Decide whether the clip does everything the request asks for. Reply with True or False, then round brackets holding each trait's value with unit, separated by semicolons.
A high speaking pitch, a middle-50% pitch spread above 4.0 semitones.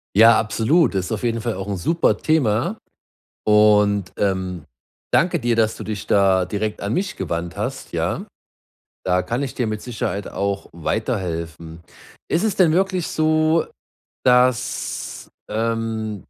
False (110 Hz; 4.5 semitones)